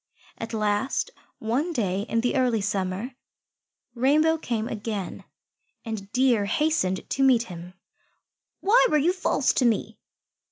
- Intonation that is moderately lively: Yes, average, 4.9 semitones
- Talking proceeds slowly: Yes, slow, 130 wpm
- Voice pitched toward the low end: No, high, 230 Hz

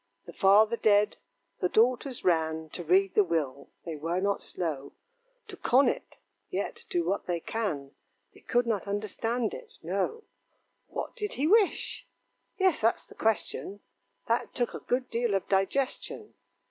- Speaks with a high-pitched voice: Yes, high, 205 Hz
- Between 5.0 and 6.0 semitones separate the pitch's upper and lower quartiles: Yes, wide, 5.6 semitones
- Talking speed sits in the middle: Yes, average, 155 wpm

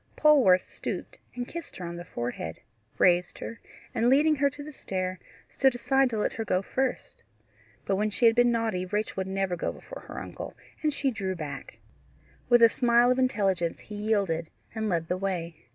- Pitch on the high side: Yes, high, 210 Hz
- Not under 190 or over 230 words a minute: Yes, average, 195 wpm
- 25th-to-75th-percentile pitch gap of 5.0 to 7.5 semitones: Yes, average, 5.3 semitones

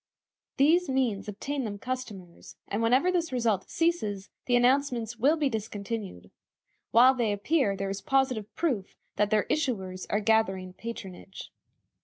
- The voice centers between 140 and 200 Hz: No, high, 230 Hz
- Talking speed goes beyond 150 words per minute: No, average, 140 wpm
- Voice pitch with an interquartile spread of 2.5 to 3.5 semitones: No, average, 4.8 semitones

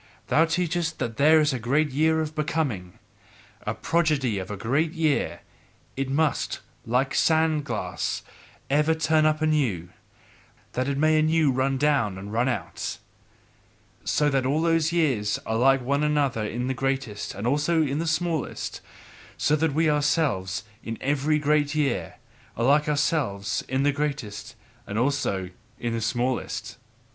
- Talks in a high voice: No, medium, 140 Hz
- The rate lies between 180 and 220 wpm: No, average, 155 wpm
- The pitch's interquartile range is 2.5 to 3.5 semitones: No, average, 4.2 semitones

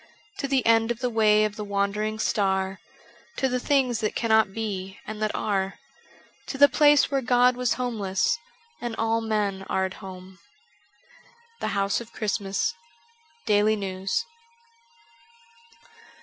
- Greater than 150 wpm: No, average, 145 wpm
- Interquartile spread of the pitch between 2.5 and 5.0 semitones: Yes, average, 3.6 semitones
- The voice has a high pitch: Yes, high, 215 Hz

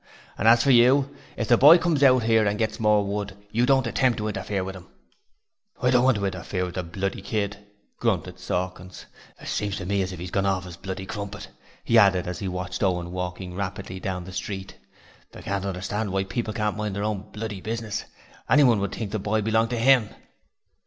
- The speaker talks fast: Yes, fast, 215 wpm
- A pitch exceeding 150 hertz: No, low, 100 Hz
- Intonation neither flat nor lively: Yes, average, 3.1 semitones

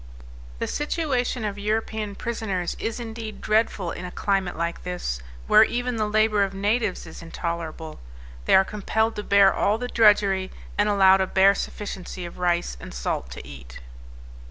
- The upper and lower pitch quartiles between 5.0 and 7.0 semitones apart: No, average, 3.6 semitones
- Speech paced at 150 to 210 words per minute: Yes, average, 165 wpm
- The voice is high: Yes, high, 200 Hz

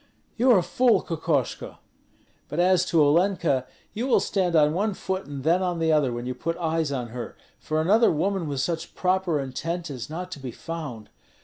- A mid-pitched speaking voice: Yes, medium, 165 Hz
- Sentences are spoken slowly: No, average, 200 wpm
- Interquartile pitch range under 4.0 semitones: No, average, 4.4 semitones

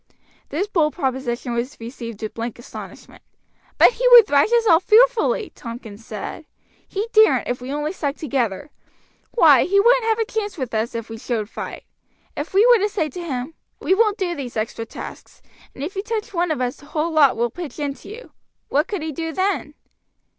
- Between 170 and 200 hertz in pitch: No, very high, 305 Hz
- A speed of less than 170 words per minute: No, average, 200 wpm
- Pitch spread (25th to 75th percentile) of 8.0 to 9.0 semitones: Yes, wide, 8.6 semitones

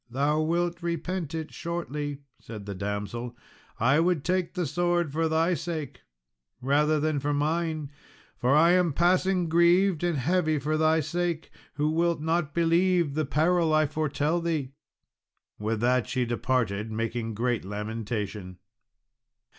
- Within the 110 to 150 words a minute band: Yes, average, 140 wpm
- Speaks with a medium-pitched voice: Yes, medium, 155 Hz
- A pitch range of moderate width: Yes, average, 5.0 semitones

